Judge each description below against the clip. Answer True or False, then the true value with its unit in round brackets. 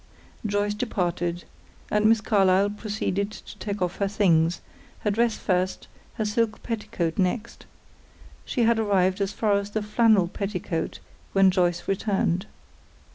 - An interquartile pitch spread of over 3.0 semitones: False (2.6 semitones)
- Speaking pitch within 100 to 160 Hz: False (200 Hz)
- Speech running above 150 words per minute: False (135 wpm)